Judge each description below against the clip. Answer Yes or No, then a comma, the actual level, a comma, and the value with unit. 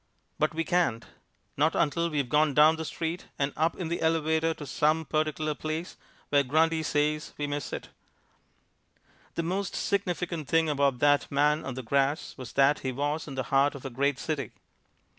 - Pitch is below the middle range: No, medium, 150 Hz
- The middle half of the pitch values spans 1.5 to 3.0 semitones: Yes, narrow, 2.4 semitones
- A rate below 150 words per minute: No, average, 180 wpm